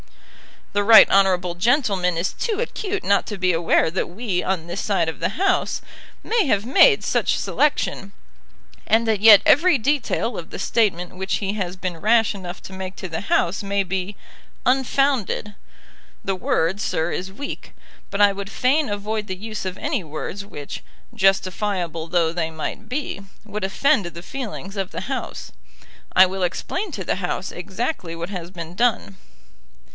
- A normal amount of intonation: Yes, average, 3.9 semitones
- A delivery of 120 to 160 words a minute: No, average, 170 wpm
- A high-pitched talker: Yes, high, 195 Hz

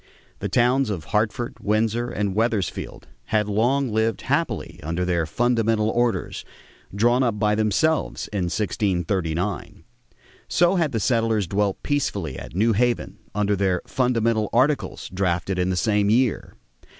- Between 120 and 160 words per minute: Yes, average, 140 wpm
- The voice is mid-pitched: No, low, 110 Hz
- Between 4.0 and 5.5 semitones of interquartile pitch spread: No, average, 3.5 semitones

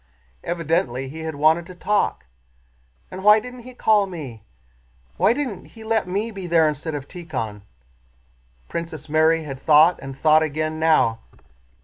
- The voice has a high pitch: No, medium, 160 Hz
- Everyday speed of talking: Yes, average, 150 wpm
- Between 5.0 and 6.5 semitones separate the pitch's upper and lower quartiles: No, average, 4.2 semitones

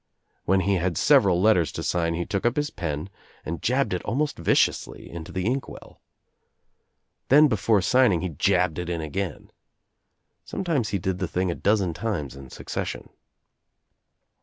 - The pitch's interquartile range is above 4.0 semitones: Yes, average, 4.8 semitones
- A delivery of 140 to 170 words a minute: Yes, average, 160 wpm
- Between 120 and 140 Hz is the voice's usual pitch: No, very low, 95 Hz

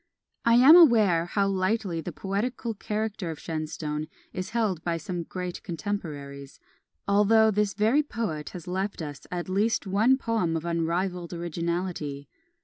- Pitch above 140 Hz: Yes, medium, 185 Hz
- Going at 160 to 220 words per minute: No, average, 140 wpm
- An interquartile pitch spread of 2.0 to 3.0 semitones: No, average, 4.4 semitones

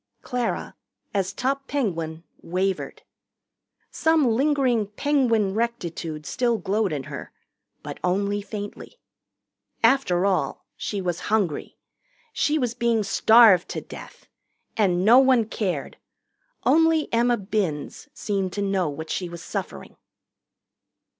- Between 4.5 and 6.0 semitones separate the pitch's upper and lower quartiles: Yes, average, 4.8 semitones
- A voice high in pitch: Yes, high, 210 Hz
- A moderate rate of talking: No, slow, 115 wpm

